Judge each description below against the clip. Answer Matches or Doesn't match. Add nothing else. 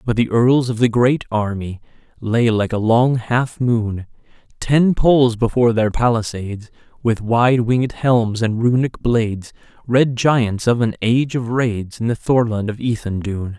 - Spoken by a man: Matches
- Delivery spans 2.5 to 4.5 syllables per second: Matches